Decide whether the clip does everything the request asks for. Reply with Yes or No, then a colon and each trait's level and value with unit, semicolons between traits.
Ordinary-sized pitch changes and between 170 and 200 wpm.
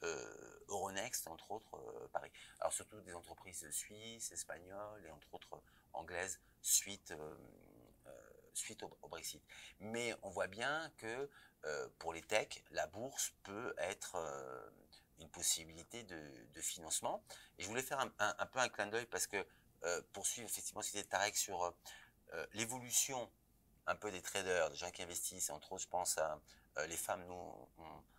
No: wide, 6.0 semitones; average, 175 wpm